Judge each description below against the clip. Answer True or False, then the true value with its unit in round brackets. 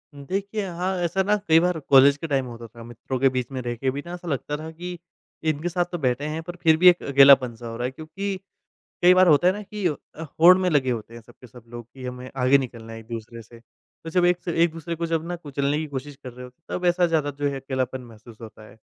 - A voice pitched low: False (145 Hz)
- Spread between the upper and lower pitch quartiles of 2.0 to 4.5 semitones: False (5.6 semitones)